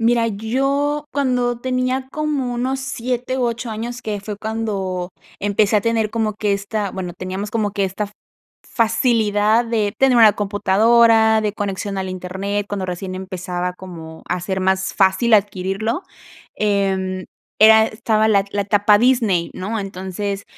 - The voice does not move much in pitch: No, average, 3.3 semitones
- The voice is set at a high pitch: Yes, high, 210 Hz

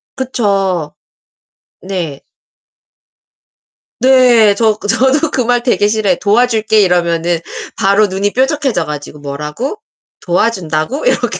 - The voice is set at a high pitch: Yes, high, 205 Hz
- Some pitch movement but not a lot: No, wide, 5.9 semitones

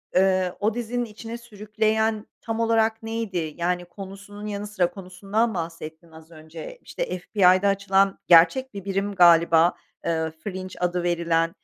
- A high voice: Yes, high, 195 Hz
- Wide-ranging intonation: No, average, 3.8 semitones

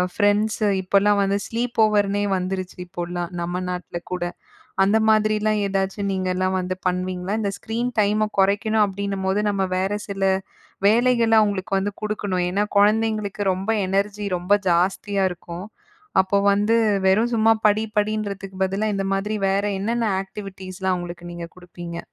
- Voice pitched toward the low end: No, high, 200 Hz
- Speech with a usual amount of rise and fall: No, narrow, 2.3 semitones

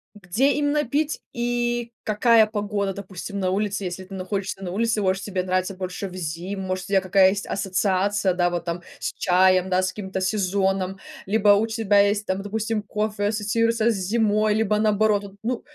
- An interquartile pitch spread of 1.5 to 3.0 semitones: Yes, narrow, 2.5 semitones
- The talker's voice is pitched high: Yes, high, 200 Hz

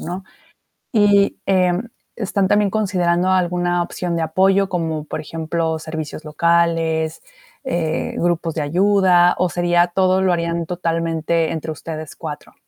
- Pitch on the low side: No, medium, 175 Hz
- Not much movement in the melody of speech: Yes, narrow, 2.3 semitones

